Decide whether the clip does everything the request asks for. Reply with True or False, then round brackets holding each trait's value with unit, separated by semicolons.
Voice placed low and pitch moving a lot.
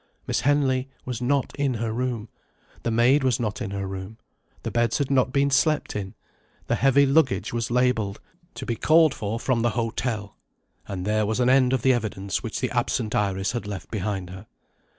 False (120 Hz; 3.8 semitones)